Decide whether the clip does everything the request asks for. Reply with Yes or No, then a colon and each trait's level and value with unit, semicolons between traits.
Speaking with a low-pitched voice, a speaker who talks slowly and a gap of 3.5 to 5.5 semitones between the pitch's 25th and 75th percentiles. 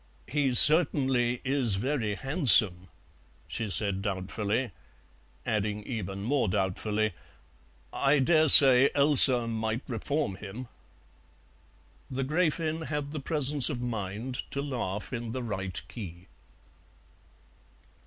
Yes: low, 120 Hz; slow, 110 wpm; average, 5.1 semitones